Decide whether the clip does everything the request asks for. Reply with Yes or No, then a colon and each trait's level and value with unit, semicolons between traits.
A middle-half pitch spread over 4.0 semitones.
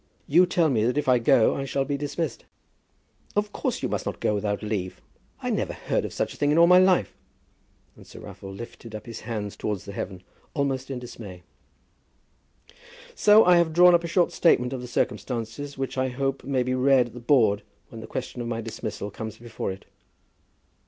Yes: average, 4.8 semitones